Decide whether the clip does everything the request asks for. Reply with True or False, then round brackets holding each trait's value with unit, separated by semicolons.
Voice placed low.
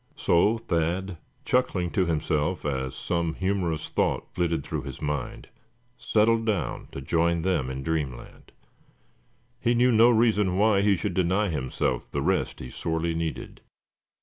True (85 Hz)